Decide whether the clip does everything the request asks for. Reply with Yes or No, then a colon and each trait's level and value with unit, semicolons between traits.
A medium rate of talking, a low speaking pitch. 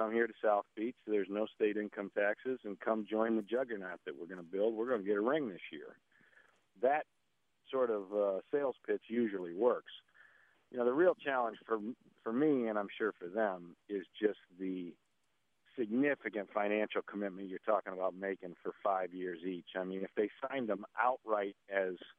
Yes: average, 195 wpm; low, 105 Hz